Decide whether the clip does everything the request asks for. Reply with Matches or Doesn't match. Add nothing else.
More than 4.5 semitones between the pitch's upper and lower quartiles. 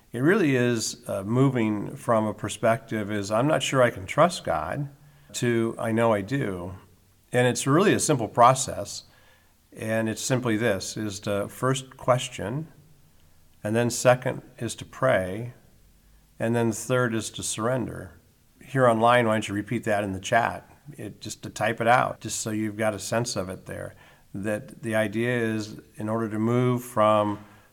Doesn't match